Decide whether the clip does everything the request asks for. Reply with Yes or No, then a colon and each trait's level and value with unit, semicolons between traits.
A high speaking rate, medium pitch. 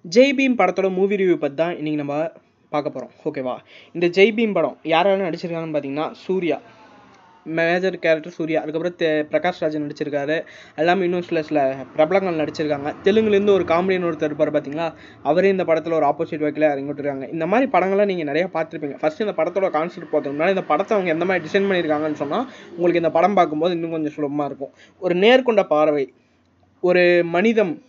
Yes: fast, 165 wpm; medium, 165 Hz